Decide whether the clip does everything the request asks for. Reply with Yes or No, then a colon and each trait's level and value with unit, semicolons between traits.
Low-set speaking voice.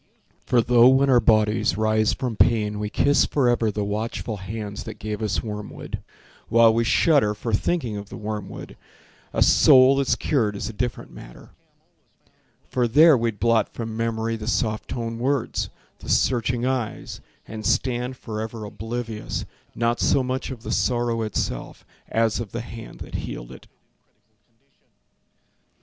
Yes: low, 115 Hz